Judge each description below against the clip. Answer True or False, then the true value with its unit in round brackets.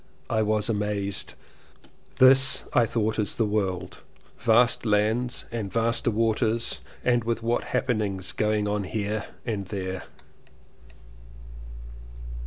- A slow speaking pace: True (110 wpm)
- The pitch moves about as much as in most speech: False (2.2 semitones)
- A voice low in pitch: True (110 Hz)